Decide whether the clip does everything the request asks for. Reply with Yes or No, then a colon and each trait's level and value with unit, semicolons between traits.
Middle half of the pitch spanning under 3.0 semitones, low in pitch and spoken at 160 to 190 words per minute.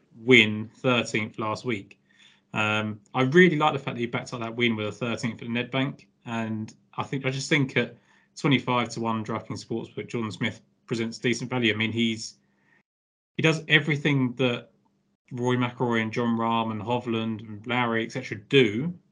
Yes: narrow, 2.6 semitones; low, 120 Hz; average, 180 wpm